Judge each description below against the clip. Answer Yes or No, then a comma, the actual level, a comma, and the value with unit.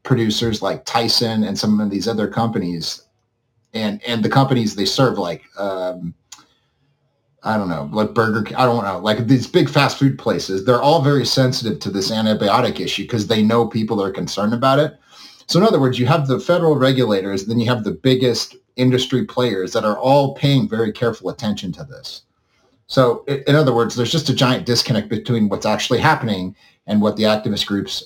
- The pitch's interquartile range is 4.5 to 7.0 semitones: No, average, 3.3 semitones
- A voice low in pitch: Yes, low, 115 Hz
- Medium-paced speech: Yes, average, 190 wpm